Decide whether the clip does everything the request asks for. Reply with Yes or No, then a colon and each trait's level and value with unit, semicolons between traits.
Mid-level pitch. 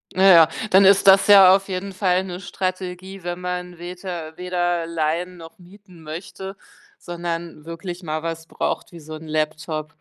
Yes: medium, 175 Hz